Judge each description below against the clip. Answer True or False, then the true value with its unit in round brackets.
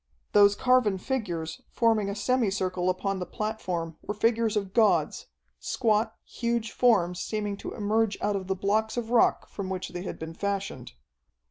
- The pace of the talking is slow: False (165 wpm)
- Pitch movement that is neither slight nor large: True (3.1 semitones)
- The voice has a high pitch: True (205 Hz)